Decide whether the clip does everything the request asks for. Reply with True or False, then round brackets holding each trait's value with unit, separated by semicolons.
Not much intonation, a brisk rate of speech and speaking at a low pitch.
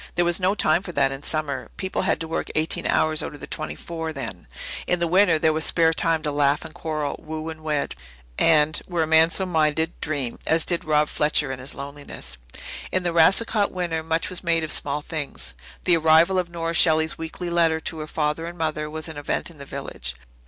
False (1.9 semitones; 225 wpm; 160 Hz)